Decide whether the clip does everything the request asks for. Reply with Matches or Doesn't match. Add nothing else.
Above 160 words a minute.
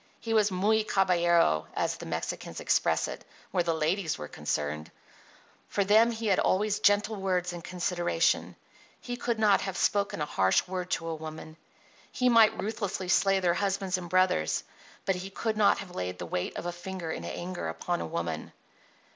Matches